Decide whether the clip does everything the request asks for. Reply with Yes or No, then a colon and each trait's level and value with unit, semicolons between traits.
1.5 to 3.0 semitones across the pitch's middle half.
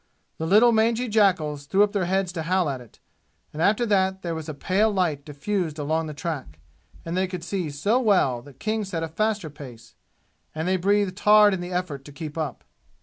No: average, 4.9 semitones